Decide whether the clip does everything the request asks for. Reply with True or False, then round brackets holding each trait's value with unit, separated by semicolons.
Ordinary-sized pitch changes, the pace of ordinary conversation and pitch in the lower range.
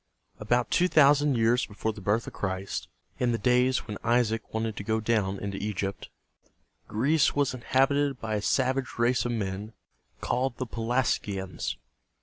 True (3.6 semitones; 165 wpm; 115 Hz)